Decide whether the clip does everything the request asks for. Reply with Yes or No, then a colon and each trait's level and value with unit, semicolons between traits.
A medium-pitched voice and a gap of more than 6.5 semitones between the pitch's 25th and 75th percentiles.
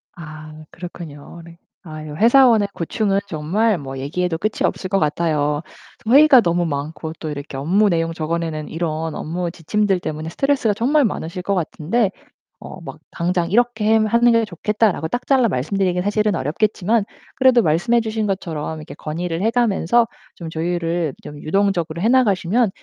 No: medium, 180 Hz; average, 5.3 semitones